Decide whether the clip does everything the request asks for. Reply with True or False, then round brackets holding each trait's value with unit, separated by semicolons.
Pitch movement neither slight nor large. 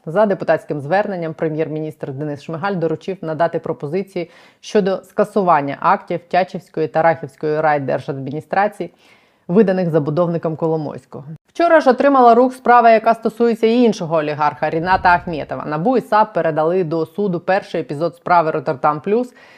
True (4.4 semitones)